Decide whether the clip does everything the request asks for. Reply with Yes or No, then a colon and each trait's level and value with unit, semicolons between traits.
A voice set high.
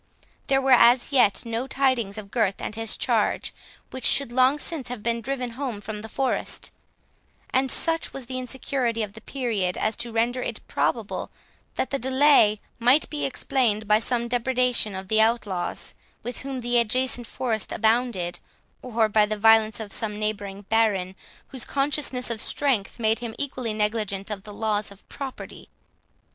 Yes: high, 230 Hz